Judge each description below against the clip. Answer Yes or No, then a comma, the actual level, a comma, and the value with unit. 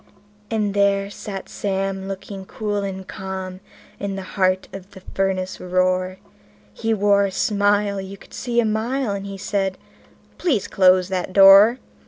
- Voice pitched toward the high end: Yes, high, 195 Hz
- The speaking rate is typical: Yes, average, 160 wpm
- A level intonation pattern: Yes, narrow, 1.3 semitones